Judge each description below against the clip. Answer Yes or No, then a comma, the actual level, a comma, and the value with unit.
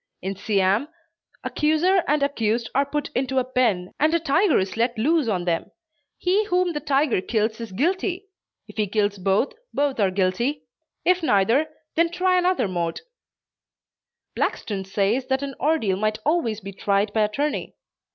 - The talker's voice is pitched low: No, very high, 250 Hz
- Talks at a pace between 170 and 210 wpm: No, average, 160 wpm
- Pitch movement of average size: No, wide, 7.1 semitones